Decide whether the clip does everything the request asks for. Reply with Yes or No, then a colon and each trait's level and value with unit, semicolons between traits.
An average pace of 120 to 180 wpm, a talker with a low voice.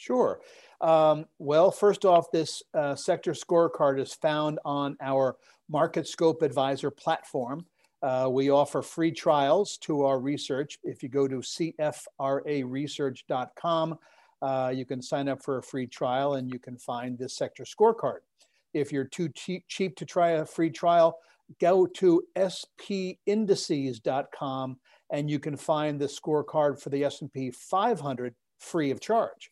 No: average, 145 wpm; medium, 150 Hz